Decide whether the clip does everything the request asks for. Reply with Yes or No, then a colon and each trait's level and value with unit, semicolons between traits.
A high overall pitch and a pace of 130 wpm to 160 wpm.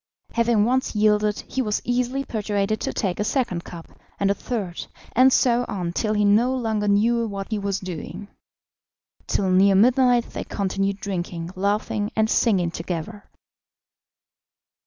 Yes: high, 210 Hz; average, 150 wpm